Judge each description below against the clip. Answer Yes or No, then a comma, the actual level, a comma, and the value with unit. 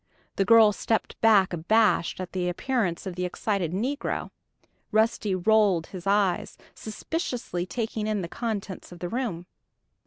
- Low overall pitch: No, high, 200 Hz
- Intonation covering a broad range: No, average, 3.7 semitones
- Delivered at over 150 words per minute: No, average, 145 wpm